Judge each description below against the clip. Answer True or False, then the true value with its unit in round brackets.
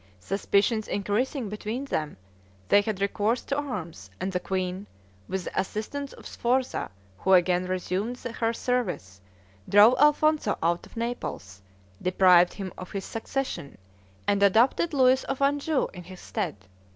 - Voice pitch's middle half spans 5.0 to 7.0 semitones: True (5.3 semitones)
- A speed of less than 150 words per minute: True (140 wpm)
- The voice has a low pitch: False (205 Hz)